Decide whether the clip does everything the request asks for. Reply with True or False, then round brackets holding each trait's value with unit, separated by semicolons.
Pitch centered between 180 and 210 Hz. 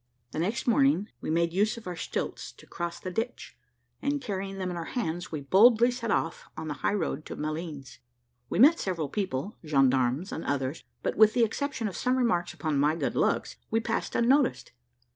True (185 Hz)